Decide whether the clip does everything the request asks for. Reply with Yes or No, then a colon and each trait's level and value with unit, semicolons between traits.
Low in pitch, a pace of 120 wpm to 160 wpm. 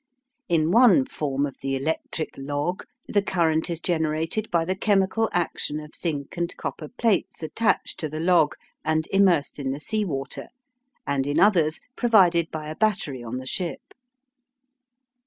No: medium, 160 Hz; average, 155 wpm